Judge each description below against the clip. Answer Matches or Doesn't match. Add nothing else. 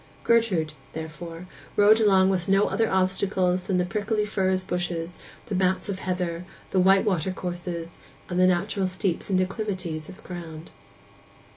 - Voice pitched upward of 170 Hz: Matches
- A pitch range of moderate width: Doesn't match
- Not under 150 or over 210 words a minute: Matches